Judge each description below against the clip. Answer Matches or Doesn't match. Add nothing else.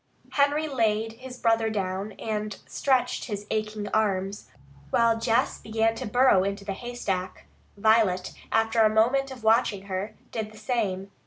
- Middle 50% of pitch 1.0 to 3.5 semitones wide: Matches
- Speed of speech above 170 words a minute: Doesn't match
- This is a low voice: Doesn't match